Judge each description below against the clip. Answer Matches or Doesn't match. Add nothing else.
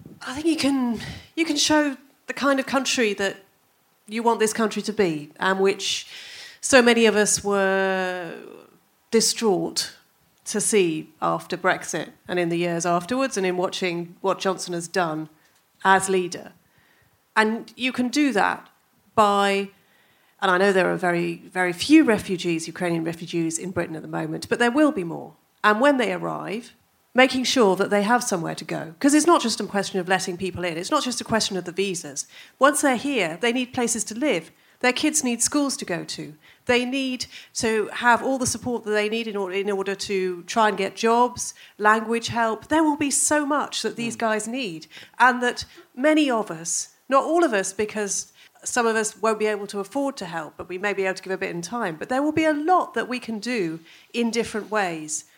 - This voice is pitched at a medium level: Doesn't match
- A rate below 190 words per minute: Doesn't match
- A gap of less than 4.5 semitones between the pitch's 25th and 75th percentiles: Doesn't match